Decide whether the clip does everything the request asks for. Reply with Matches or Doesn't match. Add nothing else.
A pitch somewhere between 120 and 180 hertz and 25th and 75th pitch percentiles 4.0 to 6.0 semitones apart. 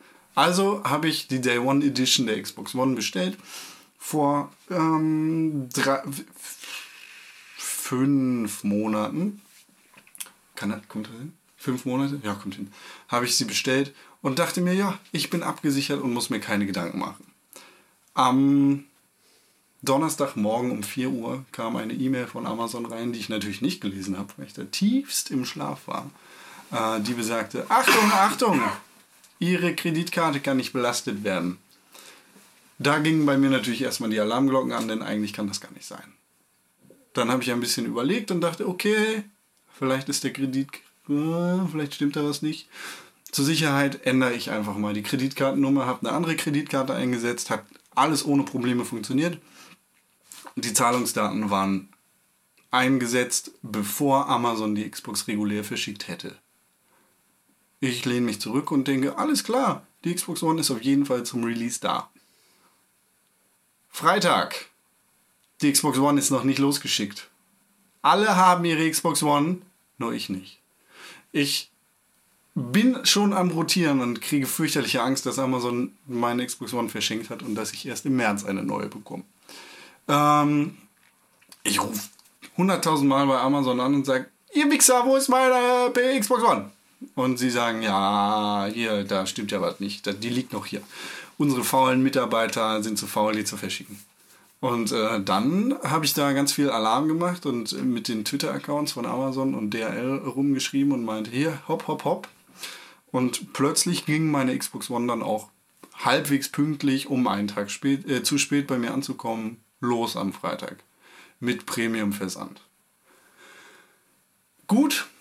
Matches